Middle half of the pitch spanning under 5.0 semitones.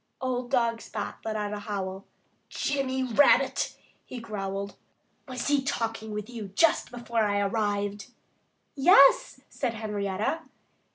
Yes: average, 3.9 semitones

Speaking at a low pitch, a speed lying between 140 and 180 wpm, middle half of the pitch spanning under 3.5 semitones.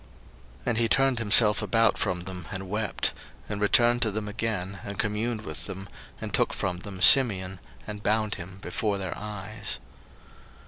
Yes: low, 105 Hz; average, 170 wpm; narrow, 2.6 semitones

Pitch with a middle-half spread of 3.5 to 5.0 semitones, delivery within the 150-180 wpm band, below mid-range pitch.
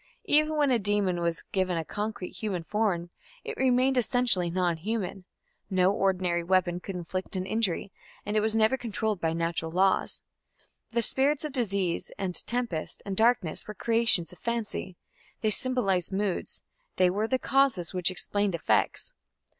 No: average, 4.2 semitones; average, 155 wpm; high, 195 Hz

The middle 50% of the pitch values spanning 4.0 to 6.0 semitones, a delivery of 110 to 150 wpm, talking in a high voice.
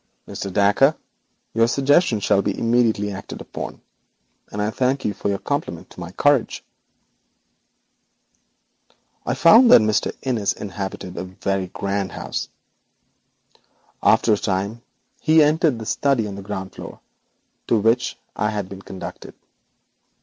No: average, 4.4 semitones; slow, 135 wpm; low, 105 Hz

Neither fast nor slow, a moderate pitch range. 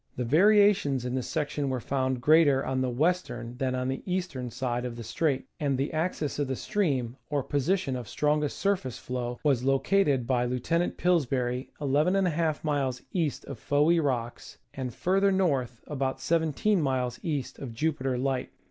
Yes: average, 165 wpm; average, 4.1 semitones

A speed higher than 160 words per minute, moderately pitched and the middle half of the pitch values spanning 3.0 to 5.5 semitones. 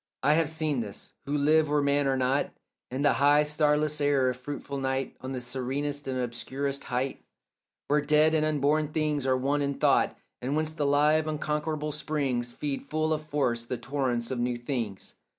No: average, 185 wpm; medium, 145 Hz; narrow, 2.6 semitones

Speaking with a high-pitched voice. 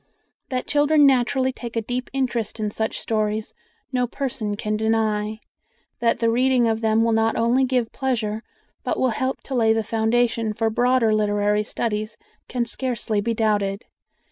Yes: high, 225 Hz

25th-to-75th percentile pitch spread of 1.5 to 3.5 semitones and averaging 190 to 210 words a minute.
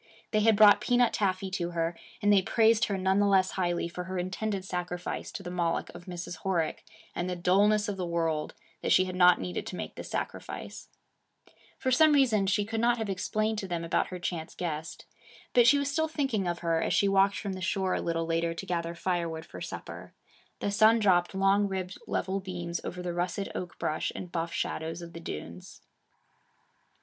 Yes: average, 2.9 semitones; fast, 205 wpm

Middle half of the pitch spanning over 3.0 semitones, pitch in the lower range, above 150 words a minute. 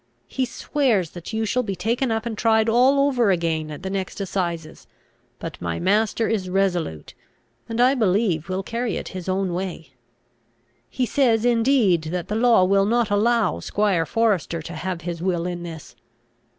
No: average, 4.7 semitones; high, 195 Hz; average, 175 wpm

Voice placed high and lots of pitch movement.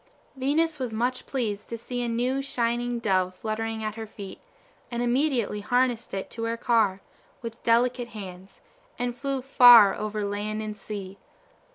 No: high, 230 Hz; average, 2.7 semitones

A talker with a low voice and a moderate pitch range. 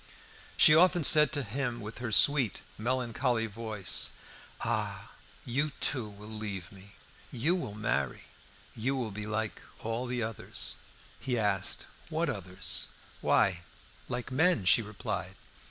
Yes: low, 115 Hz; average, 4.0 semitones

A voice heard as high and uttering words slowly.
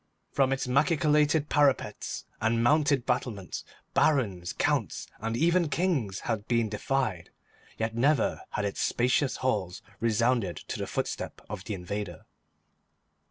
No: low, 120 Hz; slow, 125 wpm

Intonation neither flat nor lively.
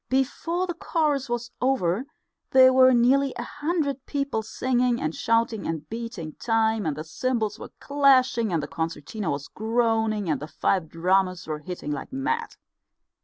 No: wide, 6.4 semitones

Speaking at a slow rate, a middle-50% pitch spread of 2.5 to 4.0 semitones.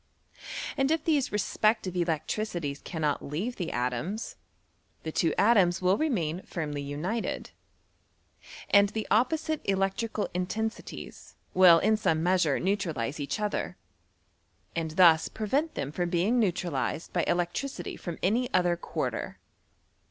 No: slow, 130 wpm; average, 5.1 semitones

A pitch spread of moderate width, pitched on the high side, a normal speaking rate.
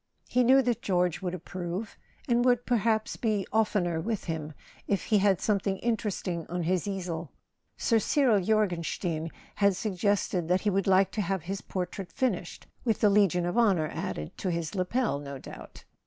Yes: average, 3.6 semitones; high, 195 Hz; average, 180 wpm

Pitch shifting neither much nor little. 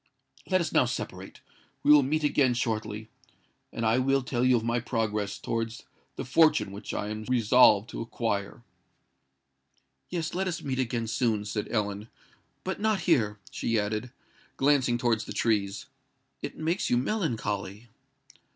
Yes: average, 4.0 semitones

